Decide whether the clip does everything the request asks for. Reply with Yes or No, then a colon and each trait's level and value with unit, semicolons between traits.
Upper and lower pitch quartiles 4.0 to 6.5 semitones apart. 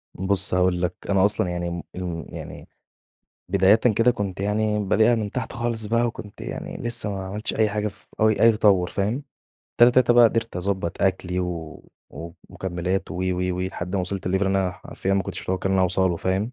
No: average, 2.9 semitones